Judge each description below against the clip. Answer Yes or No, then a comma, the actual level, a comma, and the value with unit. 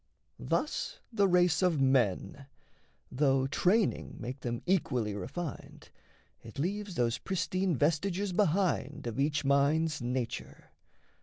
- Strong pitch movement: Yes, wide, 5.8 semitones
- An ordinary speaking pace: No, slow, 110 wpm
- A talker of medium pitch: Yes, medium, 150 Hz